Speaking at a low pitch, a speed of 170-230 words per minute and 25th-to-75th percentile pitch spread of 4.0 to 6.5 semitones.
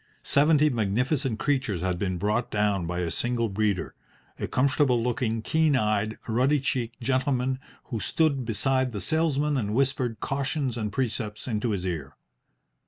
No: low, 120 Hz; average, 155 wpm; average, 4.3 semitones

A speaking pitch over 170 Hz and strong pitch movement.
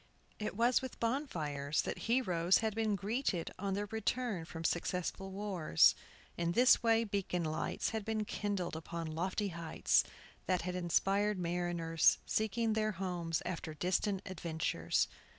No: high, 190 Hz; average, 4.2 semitones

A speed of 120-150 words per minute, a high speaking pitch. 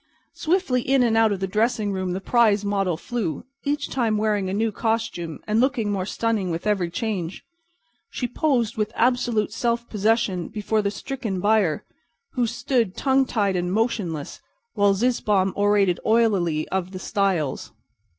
No: average, 160 wpm; high, 210 Hz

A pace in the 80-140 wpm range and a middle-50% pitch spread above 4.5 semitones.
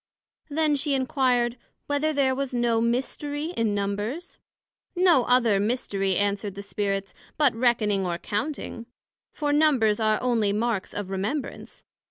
Yes: slow, 135 wpm; wide, 5.4 semitones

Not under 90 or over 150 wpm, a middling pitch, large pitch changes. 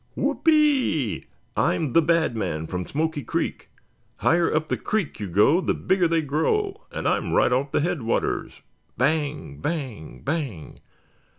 Yes: average, 140 wpm; medium, 150 Hz; wide, 5.9 semitones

